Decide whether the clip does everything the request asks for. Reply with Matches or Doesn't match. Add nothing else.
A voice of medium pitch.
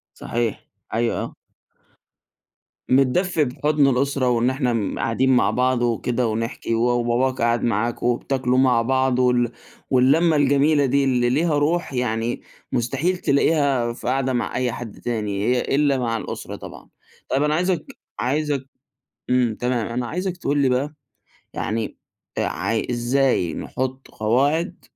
Doesn't match